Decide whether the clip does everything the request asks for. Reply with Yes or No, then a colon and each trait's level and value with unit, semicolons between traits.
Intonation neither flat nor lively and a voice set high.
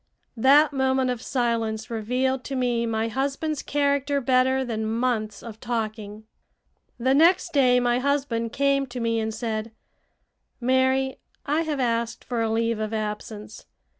Yes: average, 3.0 semitones; high, 245 Hz